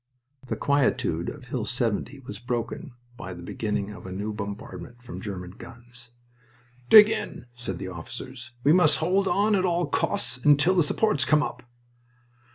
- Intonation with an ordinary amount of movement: No, wide, 6.5 semitones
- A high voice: No, low, 125 Hz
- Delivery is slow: No, average, 165 wpm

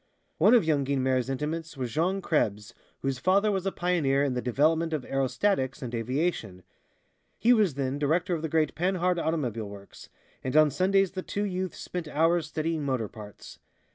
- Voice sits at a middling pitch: Yes, medium, 155 Hz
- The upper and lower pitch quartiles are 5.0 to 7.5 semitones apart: Yes, average, 5.3 semitones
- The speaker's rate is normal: Yes, average, 175 wpm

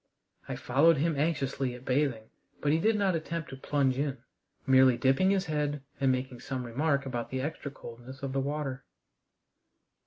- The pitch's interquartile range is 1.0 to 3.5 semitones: Yes, narrow, 2.5 semitones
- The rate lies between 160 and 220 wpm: Yes, average, 175 wpm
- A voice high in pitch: No, low, 135 Hz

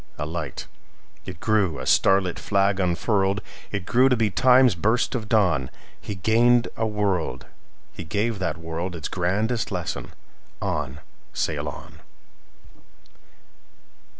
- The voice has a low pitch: Yes, very low, 95 Hz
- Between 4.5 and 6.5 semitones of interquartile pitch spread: Yes, average, 5.0 semitones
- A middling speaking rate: No, slow, 110 wpm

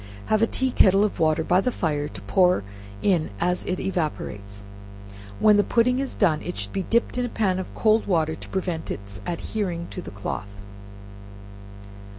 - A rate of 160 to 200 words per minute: Yes, average, 180 wpm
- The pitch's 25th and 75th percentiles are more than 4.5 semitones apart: Yes, average, 5.2 semitones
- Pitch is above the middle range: No, medium, 180 Hz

